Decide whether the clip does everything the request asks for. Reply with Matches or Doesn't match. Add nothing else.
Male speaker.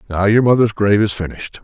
Matches